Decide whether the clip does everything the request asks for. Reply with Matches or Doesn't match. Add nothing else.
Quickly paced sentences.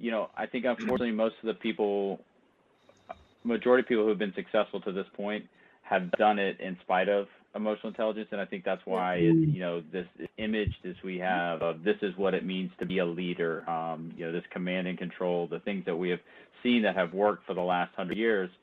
Matches